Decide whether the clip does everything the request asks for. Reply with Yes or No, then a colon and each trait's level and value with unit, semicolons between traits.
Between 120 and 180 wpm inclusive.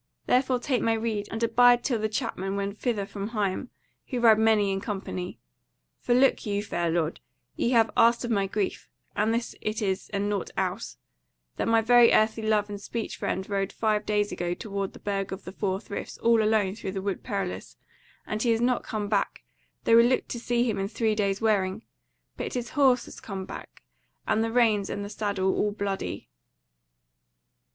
No: average, 195 wpm